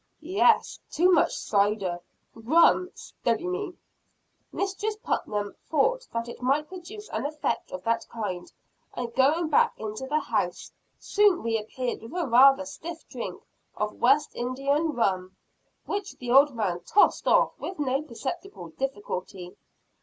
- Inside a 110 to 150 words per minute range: Yes, average, 140 wpm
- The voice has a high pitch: Yes, very high, 270 Hz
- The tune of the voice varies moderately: No, wide, 7.4 semitones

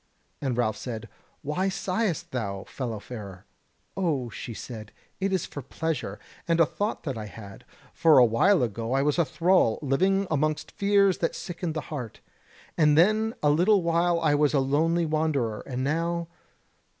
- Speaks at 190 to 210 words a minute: No, average, 170 wpm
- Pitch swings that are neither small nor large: No, wide, 5.7 semitones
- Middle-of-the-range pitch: Yes, medium, 155 Hz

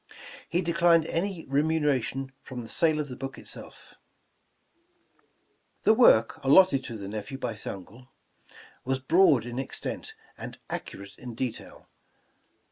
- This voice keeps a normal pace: No, slow, 130 wpm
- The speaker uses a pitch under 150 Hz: Yes, low, 135 Hz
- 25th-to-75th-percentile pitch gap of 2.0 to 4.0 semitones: No, average, 5.3 semitones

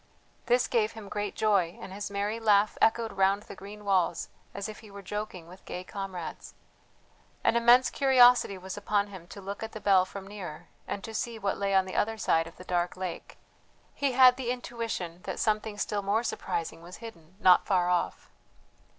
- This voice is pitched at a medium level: No, high, 200 Hz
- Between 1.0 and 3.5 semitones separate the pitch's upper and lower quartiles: Yes, average, 3.0 semitones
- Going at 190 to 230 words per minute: Yes, average, 195 wpm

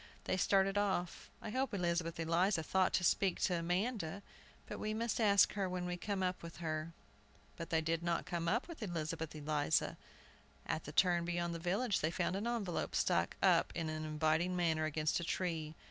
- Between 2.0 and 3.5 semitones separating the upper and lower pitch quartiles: Yes, average, 3.1 semitones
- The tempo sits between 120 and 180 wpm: No, average, 190 wpm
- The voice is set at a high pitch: No, medium, 175 Hz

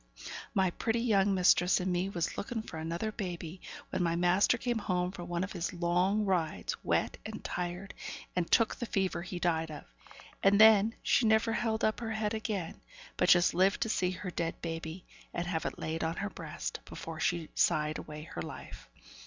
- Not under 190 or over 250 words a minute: Yes, average, 195 wpm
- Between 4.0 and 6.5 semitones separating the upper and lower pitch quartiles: No, average, 3.6 semitones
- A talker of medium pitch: Yes, medium, 180 Hz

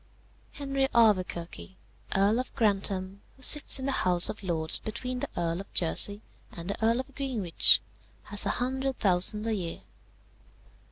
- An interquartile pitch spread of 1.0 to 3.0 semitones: No, wide, 5.4 semitones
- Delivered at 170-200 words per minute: No, average, 155 wpm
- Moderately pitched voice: No, high, 210 Hz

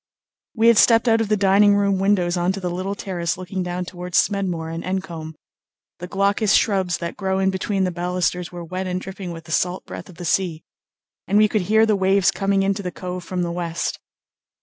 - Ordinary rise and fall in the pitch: No, narrow, 2.0 semitones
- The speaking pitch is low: No, medium, 185 Hz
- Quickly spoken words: Yes, fast, 215 wpm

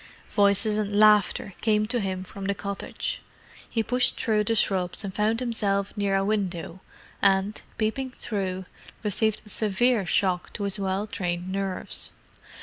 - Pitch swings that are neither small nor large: No, narrow, 2.0 semitones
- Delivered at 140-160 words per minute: Yes, average, 150 wpm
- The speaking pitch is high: Yes, high, 200 Hz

